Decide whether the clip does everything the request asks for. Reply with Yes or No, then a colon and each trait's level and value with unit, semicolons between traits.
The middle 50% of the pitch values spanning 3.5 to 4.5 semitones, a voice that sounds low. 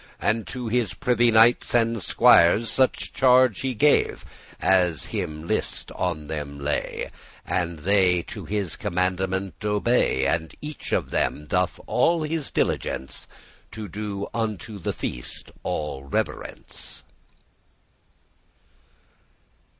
No: wide, 5.6 semitones; low, 100 Hz